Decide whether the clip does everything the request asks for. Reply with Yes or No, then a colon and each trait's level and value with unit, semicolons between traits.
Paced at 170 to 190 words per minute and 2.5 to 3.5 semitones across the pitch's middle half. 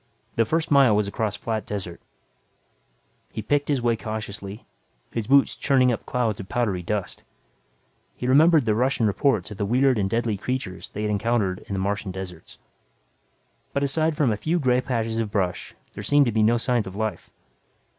No: average, 185 wpm; average, 4.1 semitones